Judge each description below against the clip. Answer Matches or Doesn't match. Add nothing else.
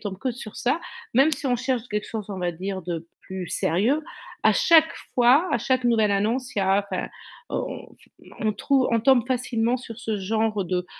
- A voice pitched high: Matches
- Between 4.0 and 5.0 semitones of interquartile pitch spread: Matches